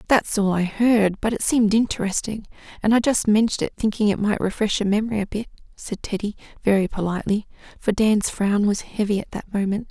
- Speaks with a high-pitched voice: Yes, high, 210 Hz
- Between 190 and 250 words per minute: Yes, average, 200 wpm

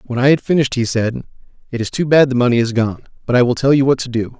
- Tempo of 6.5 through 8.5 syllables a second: Yes, 7.1 syllables/s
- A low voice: Yes, low, 125 Hz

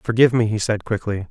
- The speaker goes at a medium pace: No, fast, 230 wpm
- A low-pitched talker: Yes, low, 110 Hz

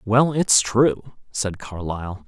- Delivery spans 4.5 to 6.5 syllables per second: No, 3.5 syllables/s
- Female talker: No, male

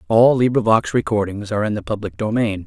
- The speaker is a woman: No, male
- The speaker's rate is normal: Yes, average, 180 wpm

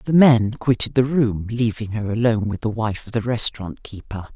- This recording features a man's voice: No, female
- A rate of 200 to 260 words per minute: Yes, fast, 205 wpm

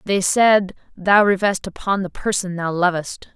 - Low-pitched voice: No, high, 190 Hz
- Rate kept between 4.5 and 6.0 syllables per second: No, 4.3 syllables/s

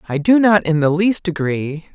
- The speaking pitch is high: No, medium, 175 Hz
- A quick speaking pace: Yes, fast, 215 wpm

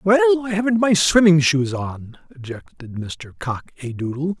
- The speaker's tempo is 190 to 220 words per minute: No, average, 165 wpm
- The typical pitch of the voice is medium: Yes, medium, 160 Hz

